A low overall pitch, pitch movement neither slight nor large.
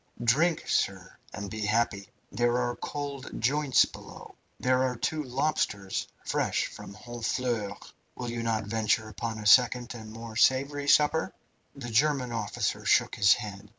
Yes: low, 120 Hz; average, 3.3 semitones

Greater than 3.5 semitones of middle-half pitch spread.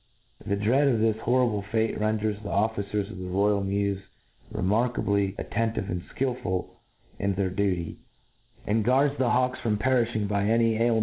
No: average, 2.7 semitones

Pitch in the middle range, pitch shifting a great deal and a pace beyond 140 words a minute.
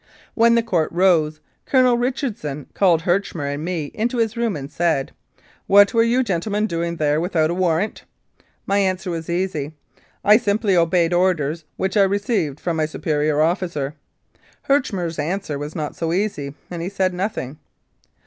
No: medium, 175 Hz; average, 4.5 semitones; average, 165 wpm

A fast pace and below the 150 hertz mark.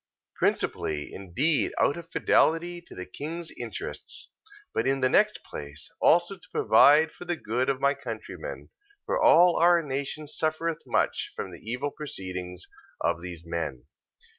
No: average, 150 wpm; medium, 140 Hz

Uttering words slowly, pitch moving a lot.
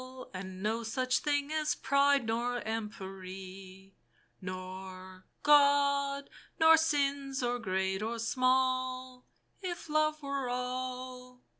Yes: slow, 105 wpm; wide, 6.3 semitones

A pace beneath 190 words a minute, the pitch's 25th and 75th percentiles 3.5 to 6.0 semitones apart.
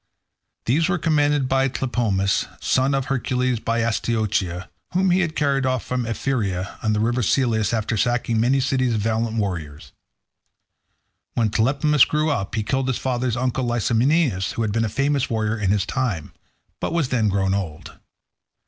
Yes: average, 165 wpm; average, 3.8 semitones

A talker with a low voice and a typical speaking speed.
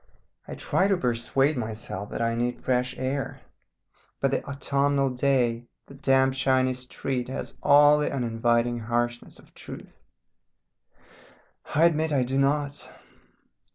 No: low, 130 Hz; slow, 130 wpm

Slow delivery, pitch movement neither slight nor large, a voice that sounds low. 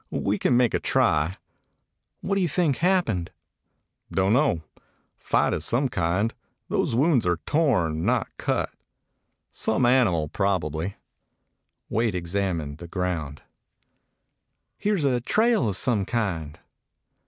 No: slow, 125 wpm; wide, 7.0 semitones; low, 100 Hz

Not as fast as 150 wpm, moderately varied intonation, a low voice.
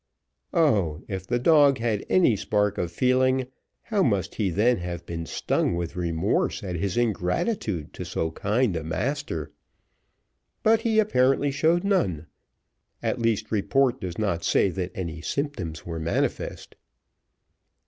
No: average, 140 wpm; wide, 7.3 semitones; low, 105 Hz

